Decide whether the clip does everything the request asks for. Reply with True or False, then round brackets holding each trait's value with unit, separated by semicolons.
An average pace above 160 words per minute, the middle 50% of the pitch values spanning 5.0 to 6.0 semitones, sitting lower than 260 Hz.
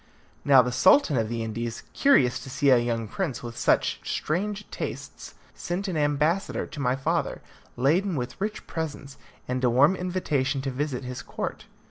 True (170 wpm; 5.5 semitones; 140 Hz)